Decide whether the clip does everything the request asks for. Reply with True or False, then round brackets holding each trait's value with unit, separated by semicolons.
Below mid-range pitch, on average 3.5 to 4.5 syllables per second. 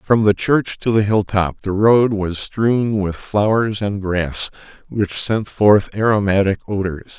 True (100 Hz; 3.8 syllables/s)